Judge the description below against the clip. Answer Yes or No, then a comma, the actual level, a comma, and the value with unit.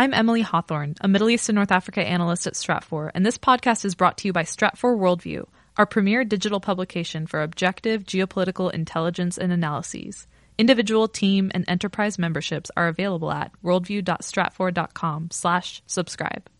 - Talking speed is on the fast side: No, average, 150 wpm